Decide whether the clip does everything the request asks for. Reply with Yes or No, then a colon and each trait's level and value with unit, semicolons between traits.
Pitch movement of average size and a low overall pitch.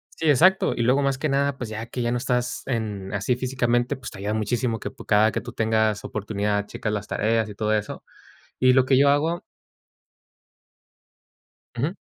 Yes: average, 3.6 semitones; low, 120 Hz